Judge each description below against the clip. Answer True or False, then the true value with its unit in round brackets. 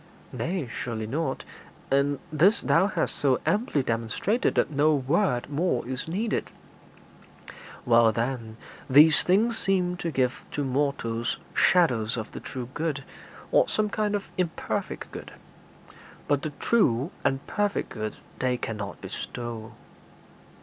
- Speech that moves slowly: True (130 wpm)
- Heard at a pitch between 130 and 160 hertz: True (140 Hz)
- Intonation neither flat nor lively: False (6.8 semitones)